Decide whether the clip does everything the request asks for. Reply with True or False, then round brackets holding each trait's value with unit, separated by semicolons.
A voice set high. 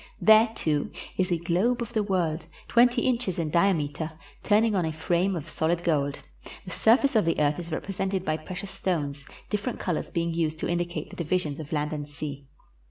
False (170 Hz)